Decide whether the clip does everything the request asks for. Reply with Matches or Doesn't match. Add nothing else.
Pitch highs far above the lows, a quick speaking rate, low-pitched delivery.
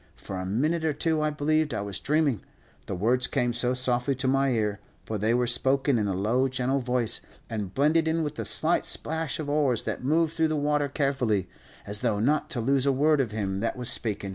Doesn't match